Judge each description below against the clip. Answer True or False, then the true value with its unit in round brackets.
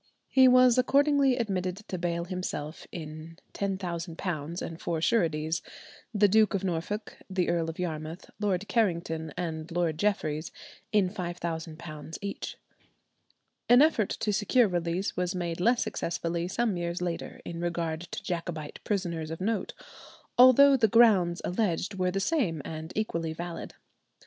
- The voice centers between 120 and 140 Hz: False (180 Hz)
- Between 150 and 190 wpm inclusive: False (135 wpm)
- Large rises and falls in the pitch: False (3.9 semitones)